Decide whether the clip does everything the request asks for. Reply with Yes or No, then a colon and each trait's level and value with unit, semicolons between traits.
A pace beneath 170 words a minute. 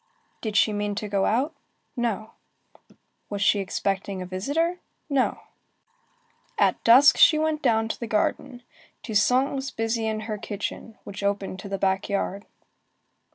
Yes: average, 150 wpm